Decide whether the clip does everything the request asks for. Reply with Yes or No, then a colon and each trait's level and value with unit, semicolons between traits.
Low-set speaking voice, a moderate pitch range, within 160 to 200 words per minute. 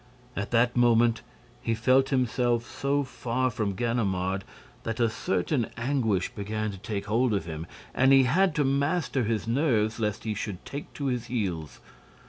Yes: low, 115 Hz; average, 3.7 semitones; average, 165 wpm